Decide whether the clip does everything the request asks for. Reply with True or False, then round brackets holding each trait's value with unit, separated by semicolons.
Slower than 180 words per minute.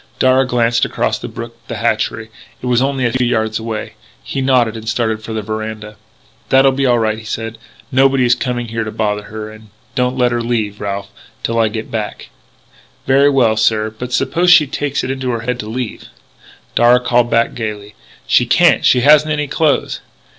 False (205 wpm)